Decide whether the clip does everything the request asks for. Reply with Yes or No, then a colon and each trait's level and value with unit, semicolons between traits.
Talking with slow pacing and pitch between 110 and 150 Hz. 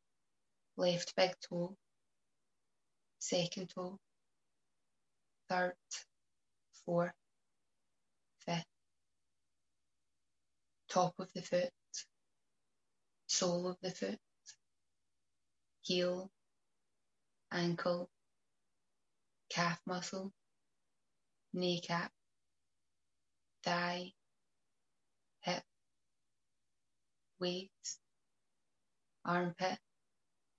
No: slow, 50 wpm; medium, 170 Hz